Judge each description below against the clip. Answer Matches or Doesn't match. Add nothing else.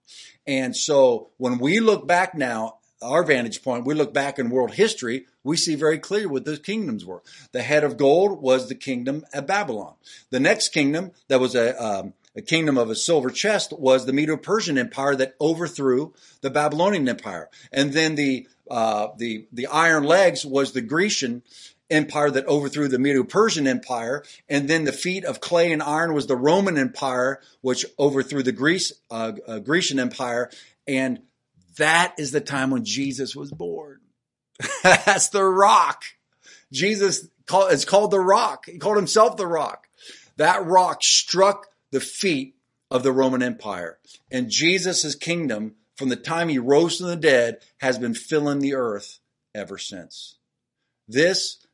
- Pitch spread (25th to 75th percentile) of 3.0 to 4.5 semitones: Doesn't match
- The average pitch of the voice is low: Doesn't match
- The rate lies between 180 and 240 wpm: Doesn't match